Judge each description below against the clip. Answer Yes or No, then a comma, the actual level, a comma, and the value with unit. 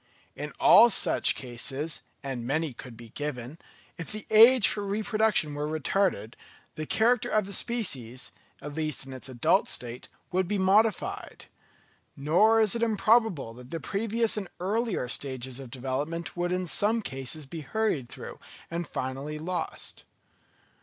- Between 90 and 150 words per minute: Yes, average, 145 wpm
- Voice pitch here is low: No, medium, 160 Hz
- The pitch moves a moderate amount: No, wide, 7.9 semitones